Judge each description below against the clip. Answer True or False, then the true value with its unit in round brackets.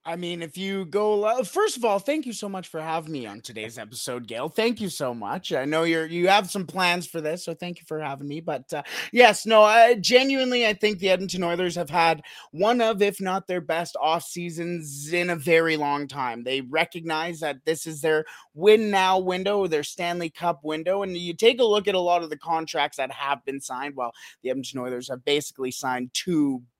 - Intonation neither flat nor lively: True (4.7 semitones)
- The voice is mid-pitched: True (170 Hz)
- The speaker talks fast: True (225 wpm)